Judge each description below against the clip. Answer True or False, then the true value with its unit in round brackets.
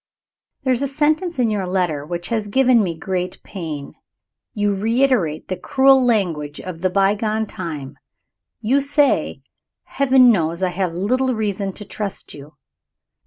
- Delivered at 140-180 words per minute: True (150 wpm)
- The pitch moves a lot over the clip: True (6.2 semitones)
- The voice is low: False (205 Hz)